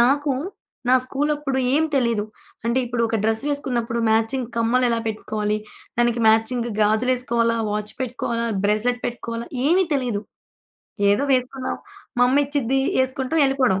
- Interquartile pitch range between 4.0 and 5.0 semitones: No, average, 2.7 semitones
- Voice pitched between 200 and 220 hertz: No, high, 240 Hz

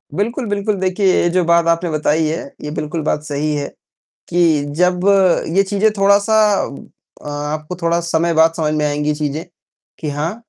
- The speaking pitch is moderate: Yes, medium, 165 Hz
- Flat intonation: No, average, 3.5 semitones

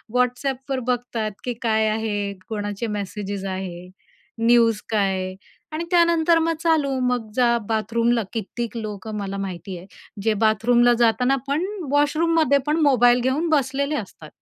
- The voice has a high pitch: Yes, high, 235 Hz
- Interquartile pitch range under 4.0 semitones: No, average, 4.8 semitones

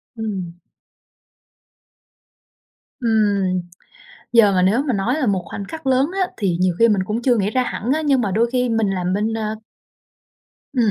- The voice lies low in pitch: No, high, 220 Hz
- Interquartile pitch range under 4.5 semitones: Yes, average, 4.1 semitones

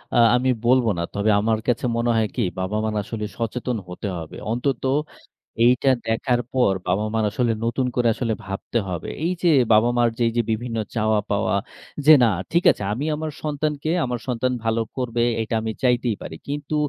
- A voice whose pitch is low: Yes, low, 120 Hz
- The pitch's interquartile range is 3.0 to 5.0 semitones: No, narrow, 2.6 semitones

